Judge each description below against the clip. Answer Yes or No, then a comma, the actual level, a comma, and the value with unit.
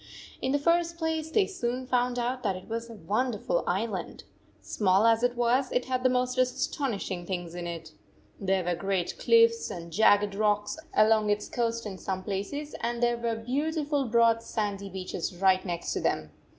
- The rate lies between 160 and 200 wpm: Yes, average, 180 wpm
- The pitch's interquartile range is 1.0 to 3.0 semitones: No, average, 4.7 semitones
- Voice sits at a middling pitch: No, high, 225 Hz